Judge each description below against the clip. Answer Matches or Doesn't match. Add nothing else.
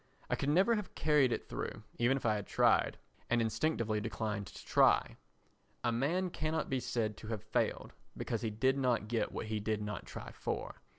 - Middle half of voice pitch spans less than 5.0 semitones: Matches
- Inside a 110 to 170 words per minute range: Doesn't match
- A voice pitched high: Doesn't match